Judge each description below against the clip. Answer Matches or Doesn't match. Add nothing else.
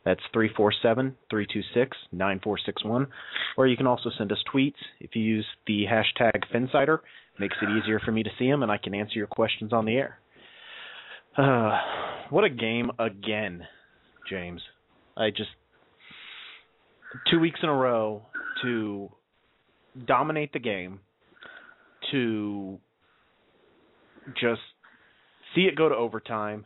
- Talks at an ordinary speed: Doesn't match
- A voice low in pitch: Matches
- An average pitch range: Matches